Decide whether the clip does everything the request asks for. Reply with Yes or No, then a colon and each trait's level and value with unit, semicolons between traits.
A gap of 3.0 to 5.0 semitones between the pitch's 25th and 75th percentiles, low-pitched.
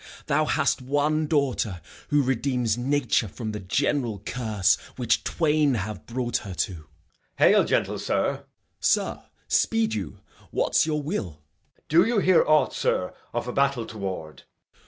No: wide, 5.5 semitones; low, 125 Hz